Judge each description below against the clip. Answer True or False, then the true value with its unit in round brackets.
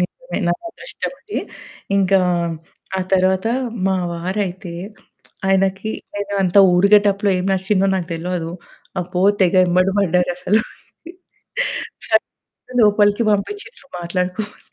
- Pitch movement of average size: False (2.3 semitones)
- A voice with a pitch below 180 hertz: False (190 Hz)